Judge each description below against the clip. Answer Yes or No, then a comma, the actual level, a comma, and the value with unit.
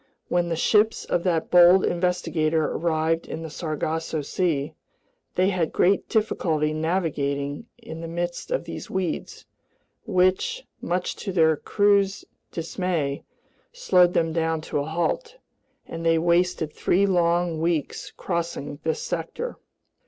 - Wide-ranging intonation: No, narrow, 2.4 semitones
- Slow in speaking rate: Yes, slow, 130 wpm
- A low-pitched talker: No, medium, 170 Hz